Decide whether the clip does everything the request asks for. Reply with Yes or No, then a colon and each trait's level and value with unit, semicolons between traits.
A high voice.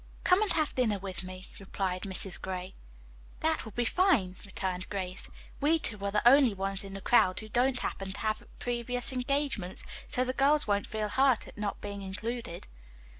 Yes: high, 210 Hz